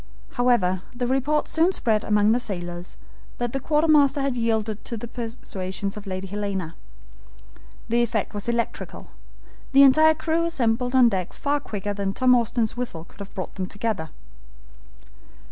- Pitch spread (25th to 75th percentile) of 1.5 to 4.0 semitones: No, average, 4.6 semitones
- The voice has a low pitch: No, high, 230 Hz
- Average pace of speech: Yes, average, 155 wpm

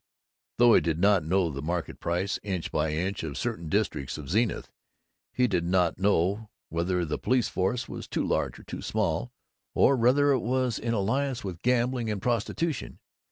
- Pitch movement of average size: No, wide, 6.0 semitones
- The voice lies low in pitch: Yes, low, 100 Hz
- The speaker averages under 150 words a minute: No, average, 175 wpm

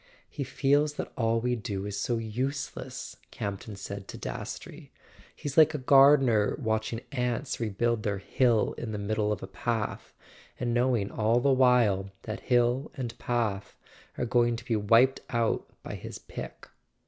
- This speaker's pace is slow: No, average, 165 wpm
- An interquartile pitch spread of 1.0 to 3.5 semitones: Yes, average, 3.1 semitones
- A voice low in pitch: Yes, low, 120 Hz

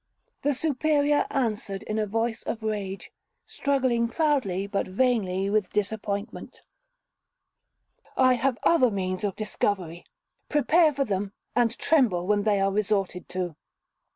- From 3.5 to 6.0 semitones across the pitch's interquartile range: Yes, average, 4.7 semitones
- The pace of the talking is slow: Yes, slow, 125 wpm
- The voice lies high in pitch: Yes, high, 215 Hz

